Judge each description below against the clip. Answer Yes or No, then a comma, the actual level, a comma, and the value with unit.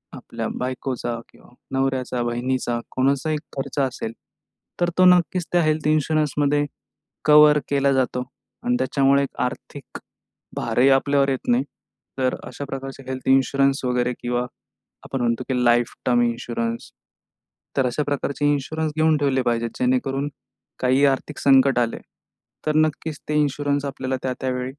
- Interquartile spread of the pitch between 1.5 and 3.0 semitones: Yes, narrow, 2.5 semitones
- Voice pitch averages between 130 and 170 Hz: Yes, low, 135 Hz